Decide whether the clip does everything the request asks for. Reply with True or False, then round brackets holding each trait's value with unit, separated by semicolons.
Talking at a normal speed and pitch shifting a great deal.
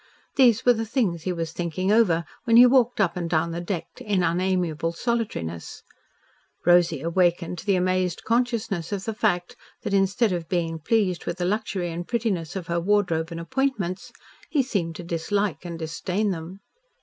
False (175 wpm; 3.9 semitones)